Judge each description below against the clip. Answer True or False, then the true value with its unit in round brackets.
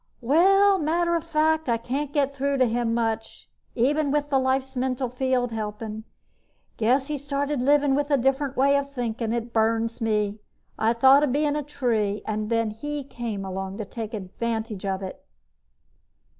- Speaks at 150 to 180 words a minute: True (170 wpm)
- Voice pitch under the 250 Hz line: False (255 Hz)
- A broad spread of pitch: False (4.2 semitones)